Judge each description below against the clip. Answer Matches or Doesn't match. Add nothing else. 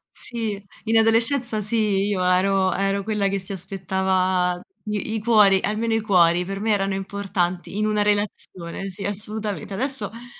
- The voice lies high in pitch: Matches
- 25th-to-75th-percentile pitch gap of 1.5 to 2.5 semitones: Matches